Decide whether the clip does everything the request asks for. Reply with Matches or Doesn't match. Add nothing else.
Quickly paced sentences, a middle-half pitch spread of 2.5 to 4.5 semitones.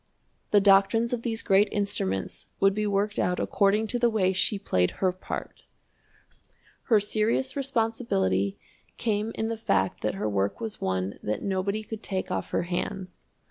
Doesn't match